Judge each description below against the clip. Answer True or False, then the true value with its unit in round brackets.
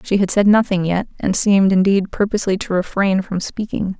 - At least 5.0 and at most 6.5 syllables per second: True (5.5 syllables/s)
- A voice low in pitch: False (195 Hz)